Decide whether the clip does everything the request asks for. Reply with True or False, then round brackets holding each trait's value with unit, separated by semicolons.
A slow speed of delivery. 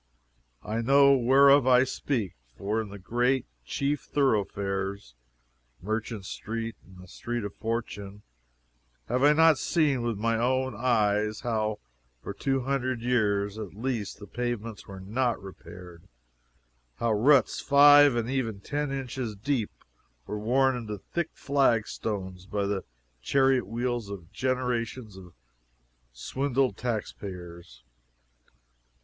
True (130 wpm)